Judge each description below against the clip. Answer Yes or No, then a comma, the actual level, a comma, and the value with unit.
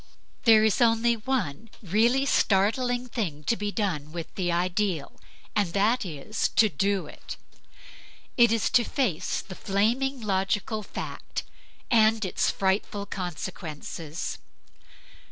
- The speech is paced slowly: Yes, slow, 120 wpm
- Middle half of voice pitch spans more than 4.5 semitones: No, average, 3.9 semitones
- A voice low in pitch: No, high, 205 Hz